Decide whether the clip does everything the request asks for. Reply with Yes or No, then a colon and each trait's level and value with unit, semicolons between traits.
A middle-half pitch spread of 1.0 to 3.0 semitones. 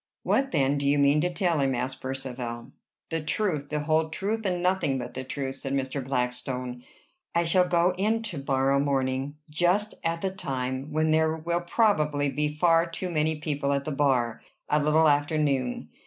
No: average, 3.9 semitones